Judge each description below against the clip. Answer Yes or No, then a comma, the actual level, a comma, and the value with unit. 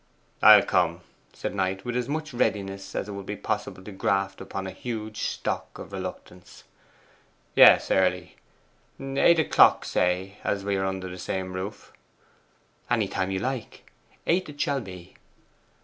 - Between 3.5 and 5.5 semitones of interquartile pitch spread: Yes, average, 4.3 semitones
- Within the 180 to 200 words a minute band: No, average, 150 wpm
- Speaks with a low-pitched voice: Yes, very low, 95 Hz